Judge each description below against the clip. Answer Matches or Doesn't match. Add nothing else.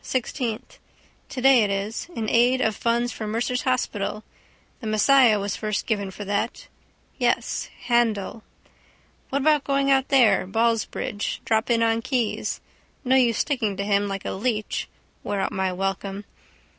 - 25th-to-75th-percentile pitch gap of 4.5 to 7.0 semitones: Doesn't match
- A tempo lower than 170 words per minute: Matches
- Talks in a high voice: Matches